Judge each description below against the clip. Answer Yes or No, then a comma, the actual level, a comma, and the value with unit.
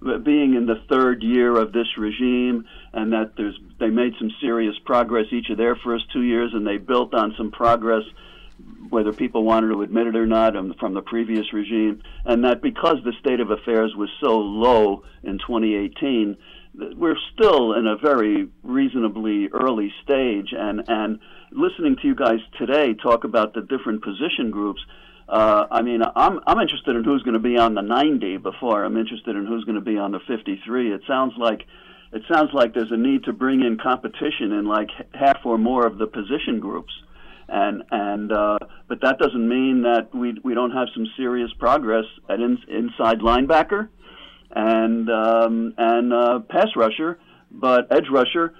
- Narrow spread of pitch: Yes, narrow, 2.3 semitones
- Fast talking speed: No, average, 185 wpm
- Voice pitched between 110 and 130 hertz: Yes, low, 115 Hz